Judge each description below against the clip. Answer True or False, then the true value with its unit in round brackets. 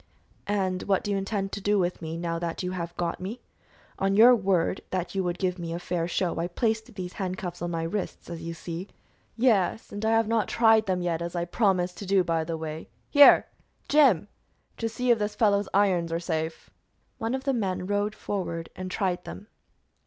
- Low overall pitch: False (185 Hz)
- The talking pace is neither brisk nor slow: False (210 wpm)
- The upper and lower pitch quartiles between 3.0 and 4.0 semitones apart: True (3.3 semitones)